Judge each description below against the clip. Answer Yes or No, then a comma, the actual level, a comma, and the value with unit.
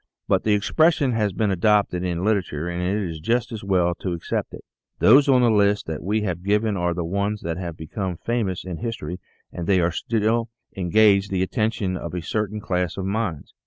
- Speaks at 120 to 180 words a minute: No, average, 200 wpm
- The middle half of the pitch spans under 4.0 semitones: Yes, average, 3.6 semitones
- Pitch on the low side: Yes, low, 100 Hz